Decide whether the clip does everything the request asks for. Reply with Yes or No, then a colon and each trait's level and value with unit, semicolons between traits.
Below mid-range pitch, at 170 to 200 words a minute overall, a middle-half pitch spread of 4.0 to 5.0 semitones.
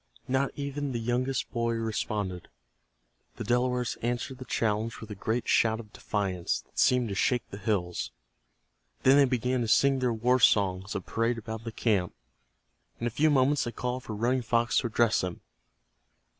No: low, 115 Hz; average, 175 wpm; average, 2.8 semitones